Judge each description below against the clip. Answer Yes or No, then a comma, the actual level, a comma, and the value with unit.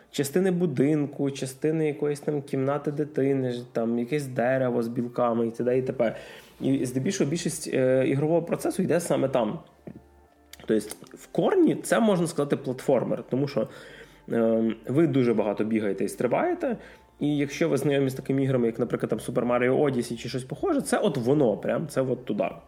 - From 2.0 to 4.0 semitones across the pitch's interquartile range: Yes, average, 3.6 semitones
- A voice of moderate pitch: No, low, 130 Hz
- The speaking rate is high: Yes, fast, 170 wpm